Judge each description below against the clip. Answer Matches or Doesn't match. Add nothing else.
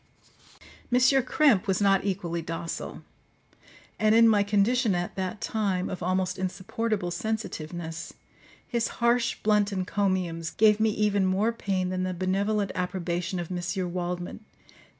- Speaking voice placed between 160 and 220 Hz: Matches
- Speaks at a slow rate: Matches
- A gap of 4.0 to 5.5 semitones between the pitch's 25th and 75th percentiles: Doesn't match